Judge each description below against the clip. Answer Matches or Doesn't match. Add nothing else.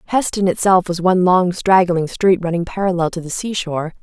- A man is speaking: Doesn't match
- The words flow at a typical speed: Matches